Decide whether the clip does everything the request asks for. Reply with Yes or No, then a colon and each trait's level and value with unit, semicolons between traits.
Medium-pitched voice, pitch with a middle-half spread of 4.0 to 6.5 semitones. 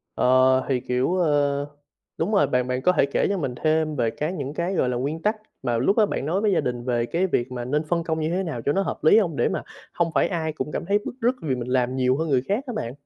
Yes: medium, 150 Hz; average, 5.3 semitones